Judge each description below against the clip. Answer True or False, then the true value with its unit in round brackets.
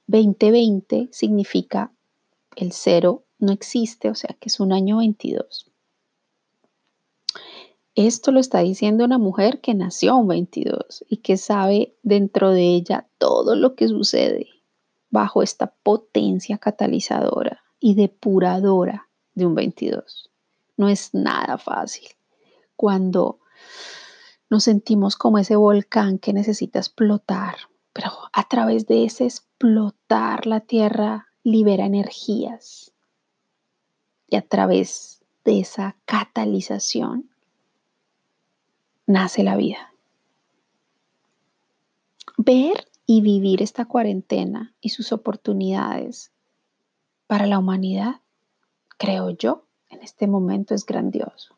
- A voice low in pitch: False (210 Hz)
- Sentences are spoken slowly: True (105 wpm)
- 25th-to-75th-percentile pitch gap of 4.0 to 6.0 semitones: False (3.3 semitones)